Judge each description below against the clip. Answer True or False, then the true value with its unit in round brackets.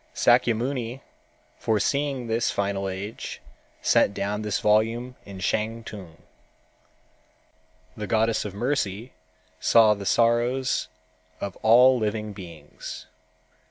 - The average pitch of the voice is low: True (110 Hz)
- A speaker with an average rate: False (95 wpm)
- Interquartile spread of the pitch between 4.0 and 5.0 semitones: False (3.0 semitones)